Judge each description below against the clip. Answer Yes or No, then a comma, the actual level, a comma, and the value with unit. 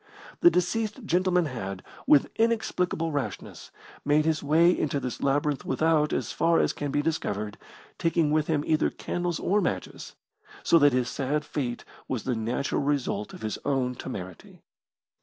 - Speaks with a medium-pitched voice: Yes, medium, 150 Hz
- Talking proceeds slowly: No, average, 160 wpm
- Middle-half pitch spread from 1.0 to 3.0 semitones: No, average, 4.4 semitones